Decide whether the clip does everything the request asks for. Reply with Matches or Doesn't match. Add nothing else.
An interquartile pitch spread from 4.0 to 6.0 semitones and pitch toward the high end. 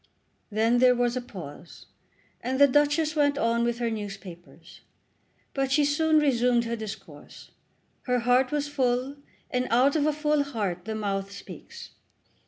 Matches